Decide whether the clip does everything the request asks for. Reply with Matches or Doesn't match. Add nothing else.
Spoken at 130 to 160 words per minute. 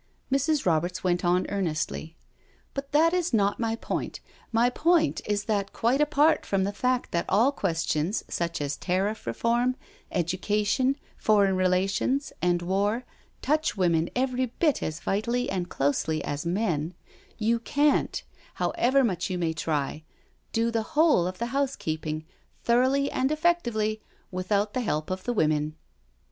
Matches